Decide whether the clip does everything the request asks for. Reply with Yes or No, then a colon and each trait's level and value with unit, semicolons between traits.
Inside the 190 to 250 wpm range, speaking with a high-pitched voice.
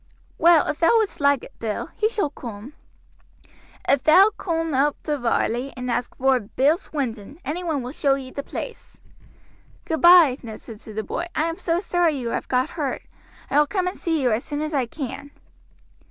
Yes: average, 195 wpm; very high, 285 Hz